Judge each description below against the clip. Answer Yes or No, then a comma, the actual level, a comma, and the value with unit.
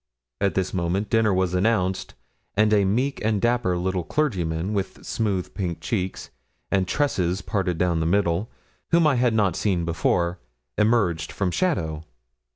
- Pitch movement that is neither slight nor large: Yes, average, 3.7 semitones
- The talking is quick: No, average, 155 wpm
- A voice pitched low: Yes, very low, 95 Hz